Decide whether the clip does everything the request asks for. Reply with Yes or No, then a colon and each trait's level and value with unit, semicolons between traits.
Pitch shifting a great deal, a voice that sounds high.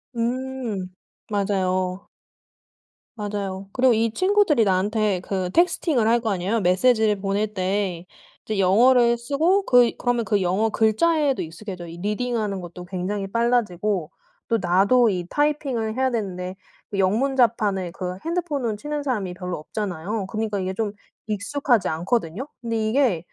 No: average, 4.5 semitones; high, 215 Hz